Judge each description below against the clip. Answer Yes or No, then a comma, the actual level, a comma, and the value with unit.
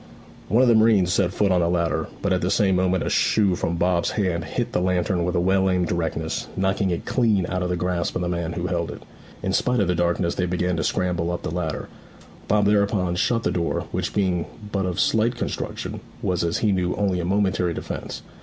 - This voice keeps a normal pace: No, fast, 230 wpm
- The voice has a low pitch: Yes, very low, 90 Hz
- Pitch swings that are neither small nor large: No, narrow, 2.2 semitones